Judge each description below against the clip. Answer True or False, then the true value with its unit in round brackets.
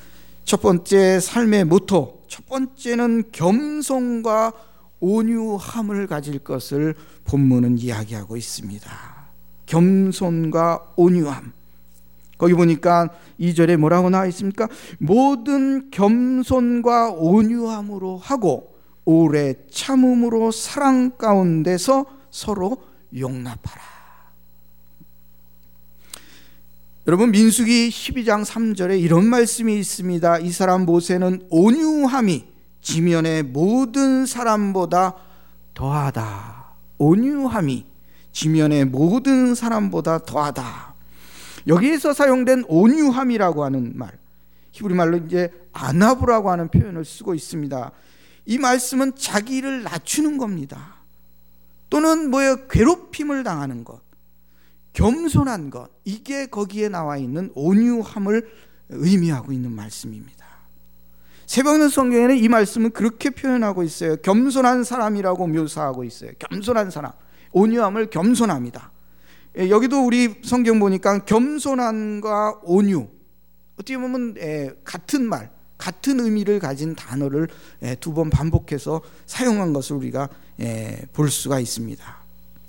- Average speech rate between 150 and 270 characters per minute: True (245 characters per minute)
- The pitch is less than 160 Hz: False (180 Hz)